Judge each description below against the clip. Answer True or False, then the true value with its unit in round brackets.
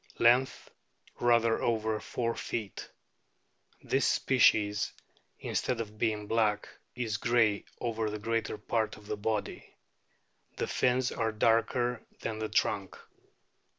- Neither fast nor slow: False (120 wpm)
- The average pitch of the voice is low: True (110 Hz)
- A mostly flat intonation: True (1.7 semitones)